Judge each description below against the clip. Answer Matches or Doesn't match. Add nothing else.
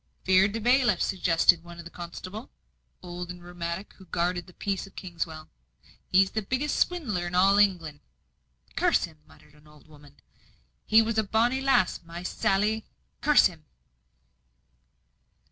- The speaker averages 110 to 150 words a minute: Matches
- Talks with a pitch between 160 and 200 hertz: Matches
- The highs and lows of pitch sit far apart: Doesn't match